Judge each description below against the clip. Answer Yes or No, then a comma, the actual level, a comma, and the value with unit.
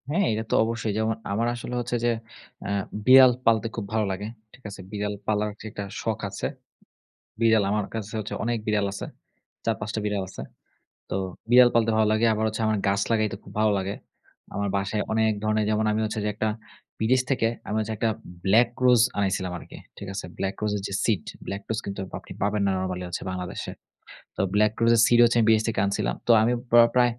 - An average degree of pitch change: No, narrow, 2.1 semitones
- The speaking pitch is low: Yes, low, 110 Hz